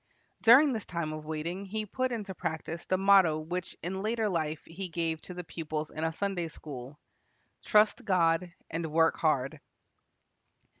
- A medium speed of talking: Yes, average, 160 wpm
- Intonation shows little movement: No, average, 3.7 semitones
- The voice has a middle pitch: Yes, medium, 170 Hz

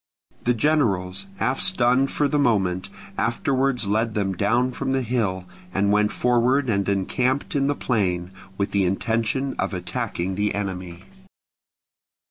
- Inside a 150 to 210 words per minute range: No, average, 140 wpm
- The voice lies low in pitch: Yes, low, 110 Hz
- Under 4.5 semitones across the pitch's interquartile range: No, average, 4.8 semitones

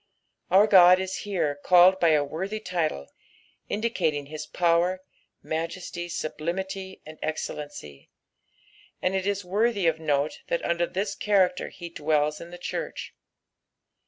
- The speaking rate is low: Yes, slow, 130 wpm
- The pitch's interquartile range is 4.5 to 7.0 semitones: No, average, 3.3 semitones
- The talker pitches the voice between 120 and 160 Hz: No, medium, 175 Hz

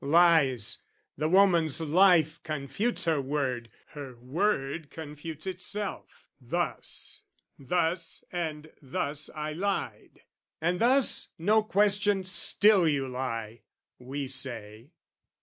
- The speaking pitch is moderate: Yes, medium, 155 Hz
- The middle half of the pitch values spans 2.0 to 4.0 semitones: No, average, 5.2 semitones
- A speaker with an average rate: No, slow, 100 wpm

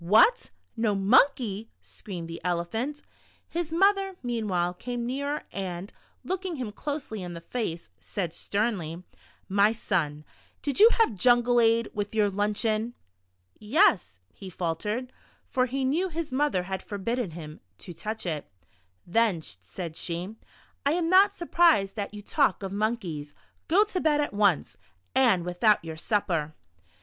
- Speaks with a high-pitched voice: Yes, high, 215 Hz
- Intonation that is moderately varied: No, wide, 6.9 semitones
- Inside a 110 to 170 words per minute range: Yes, average, 150 wpm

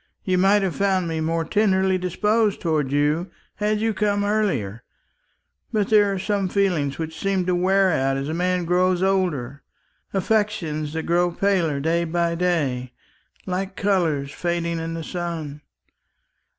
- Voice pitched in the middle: Yes, medium, 175 Hz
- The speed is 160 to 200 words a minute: No, average, 150 wpm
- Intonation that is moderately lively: Yes, average, 3.4 semitones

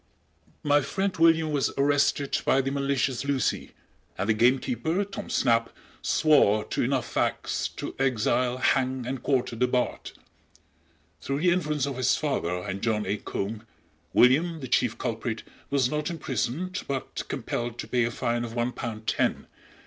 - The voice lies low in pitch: Yes, low, 130 Hz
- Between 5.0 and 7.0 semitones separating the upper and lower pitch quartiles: No, average, 3.4 semitones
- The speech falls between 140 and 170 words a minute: Yes, average, 155 wpm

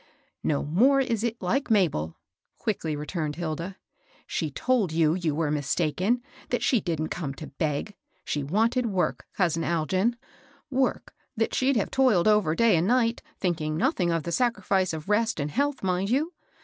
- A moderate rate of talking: Yes, average, 175 wpm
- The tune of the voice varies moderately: No, wide, 6.7 semitones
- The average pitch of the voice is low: No, medium, 185 Hz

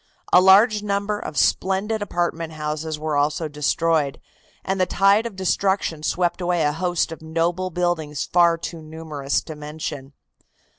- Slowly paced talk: No, average, 150 wpm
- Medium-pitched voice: Yes, medium, 165 Hz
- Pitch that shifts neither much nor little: Yes, average, 3.5 semitones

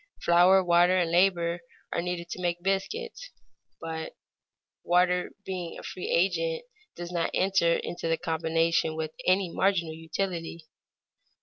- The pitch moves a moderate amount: No, narrow, 2.1 semitones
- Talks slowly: Yes, slow, 130 wpm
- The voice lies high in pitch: No, medium, 175 Hz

